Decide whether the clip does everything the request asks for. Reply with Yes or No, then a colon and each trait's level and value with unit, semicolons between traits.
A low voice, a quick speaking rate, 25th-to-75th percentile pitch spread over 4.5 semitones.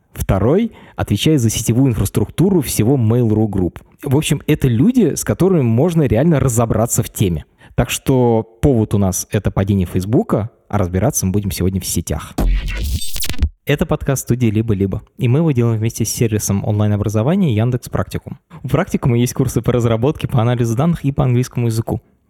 Yes: low, 115 Hz; fast, 165 wpm; average, 4.9 semitones